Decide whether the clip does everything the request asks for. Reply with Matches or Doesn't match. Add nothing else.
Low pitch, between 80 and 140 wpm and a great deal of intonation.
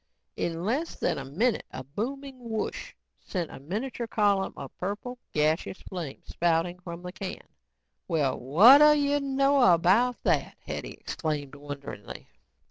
Doesn't match